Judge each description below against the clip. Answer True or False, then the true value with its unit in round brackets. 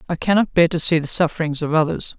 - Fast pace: True (245 wpm)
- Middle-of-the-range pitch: True (165 Hz)